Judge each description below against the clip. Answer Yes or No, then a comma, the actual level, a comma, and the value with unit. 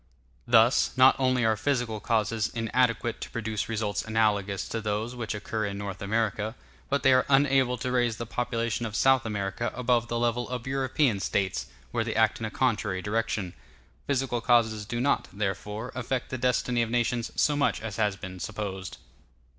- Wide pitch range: No, average, 2.7 semitones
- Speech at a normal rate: Yes, average, 180 wpm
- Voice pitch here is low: Yes, low, 115 Hz